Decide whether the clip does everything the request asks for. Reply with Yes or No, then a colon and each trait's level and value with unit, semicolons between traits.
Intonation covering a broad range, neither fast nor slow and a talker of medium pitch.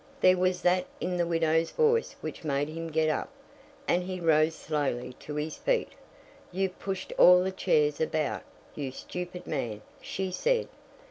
No: average, 3.2 semitones; average, 160 wpm; medium, 165 Hz